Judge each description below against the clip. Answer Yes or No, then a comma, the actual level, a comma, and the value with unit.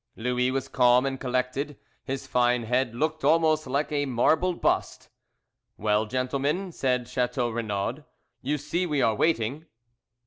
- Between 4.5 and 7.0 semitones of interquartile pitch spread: No, average, 3.3 semitones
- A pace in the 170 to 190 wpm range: No, average, 140 wpm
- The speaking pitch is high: No, low, 130 Hz